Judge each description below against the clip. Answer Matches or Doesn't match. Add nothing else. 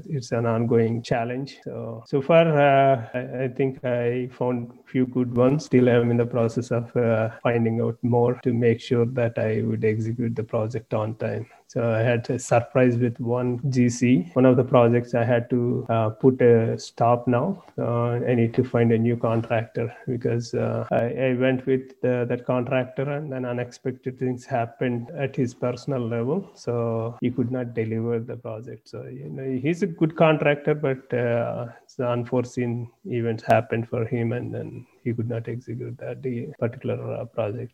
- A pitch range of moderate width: Doesn't match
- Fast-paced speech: Doesn't match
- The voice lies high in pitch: Doesn't match